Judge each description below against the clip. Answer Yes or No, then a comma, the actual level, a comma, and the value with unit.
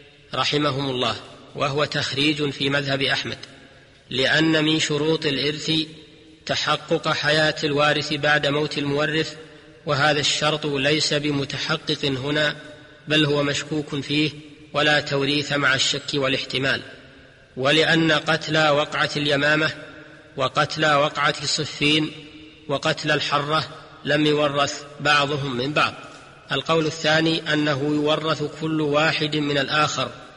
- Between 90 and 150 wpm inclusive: Yes, average, 105 wpm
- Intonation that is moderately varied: No, narrow, 1.3 semitones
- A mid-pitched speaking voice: Yes, medium, 150 Hz